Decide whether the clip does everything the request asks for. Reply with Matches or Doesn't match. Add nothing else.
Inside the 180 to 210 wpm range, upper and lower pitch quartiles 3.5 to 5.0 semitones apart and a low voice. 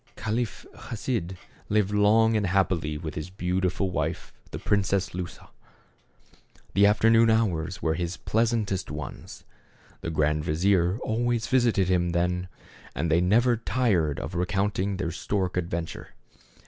Doesn't match